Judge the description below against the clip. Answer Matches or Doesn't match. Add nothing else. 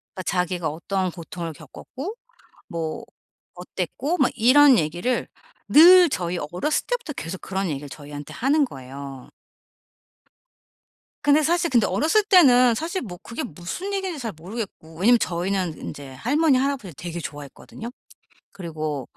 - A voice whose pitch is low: Doesn't match